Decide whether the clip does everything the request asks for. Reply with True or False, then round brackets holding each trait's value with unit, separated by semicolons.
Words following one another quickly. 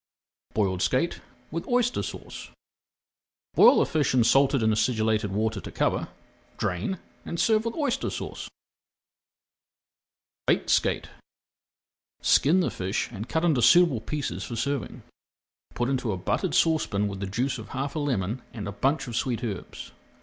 False (150 wpm)